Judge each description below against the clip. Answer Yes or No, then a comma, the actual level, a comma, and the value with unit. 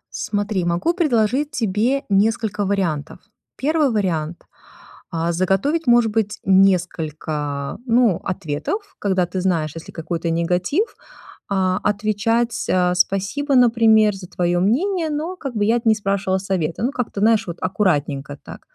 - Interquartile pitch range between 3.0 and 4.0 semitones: No, average, 4.8 semitones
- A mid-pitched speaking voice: No, high, 200 Hz